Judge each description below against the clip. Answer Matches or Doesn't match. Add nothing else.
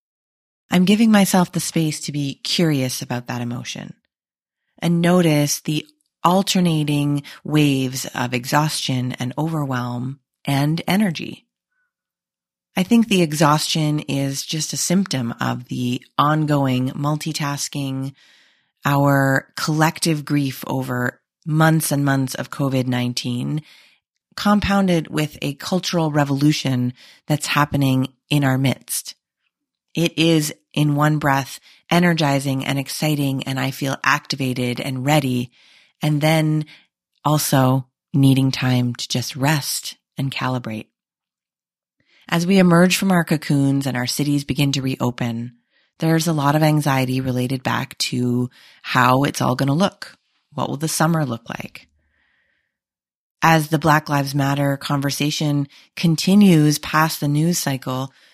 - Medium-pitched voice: Matches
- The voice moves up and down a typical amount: Matches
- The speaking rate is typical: Doesn't match